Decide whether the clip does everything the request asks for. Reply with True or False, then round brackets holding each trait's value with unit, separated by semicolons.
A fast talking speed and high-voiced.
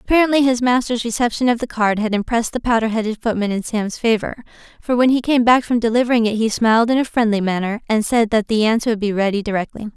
True (235 wpm; 225 Hz)